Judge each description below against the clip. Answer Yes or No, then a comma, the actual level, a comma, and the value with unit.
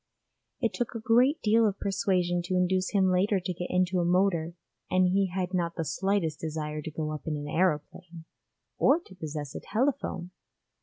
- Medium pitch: Yes, medium, 180 Hz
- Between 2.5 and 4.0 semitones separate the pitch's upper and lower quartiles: Yes, average, 3.2 semitones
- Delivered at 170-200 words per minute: Yes, average, 190 wpm